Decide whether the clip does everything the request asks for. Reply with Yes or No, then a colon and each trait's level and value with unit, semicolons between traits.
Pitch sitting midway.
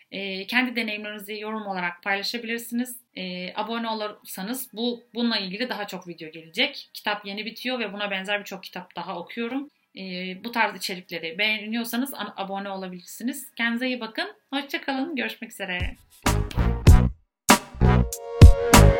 No: high, 210 Hz